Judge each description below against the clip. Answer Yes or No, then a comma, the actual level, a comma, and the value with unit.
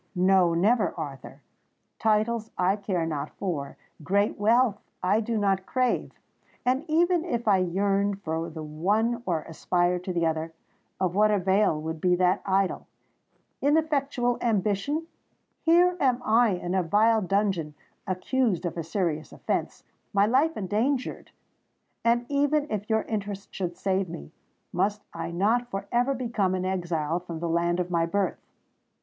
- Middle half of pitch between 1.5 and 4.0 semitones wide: No, average, 4.9 semitones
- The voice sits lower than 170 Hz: No, high, 195 Hz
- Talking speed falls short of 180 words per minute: Yes, average, 140 wpm